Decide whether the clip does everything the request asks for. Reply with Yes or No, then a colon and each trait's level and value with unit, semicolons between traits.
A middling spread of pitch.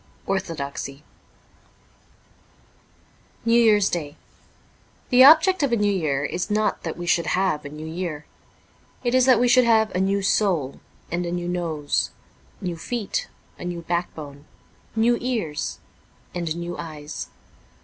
No: wide, 5.8 semitones